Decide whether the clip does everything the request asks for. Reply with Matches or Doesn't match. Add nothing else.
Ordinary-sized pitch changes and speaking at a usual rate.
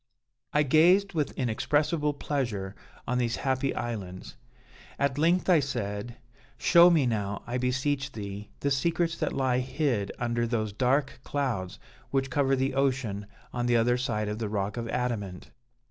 Matches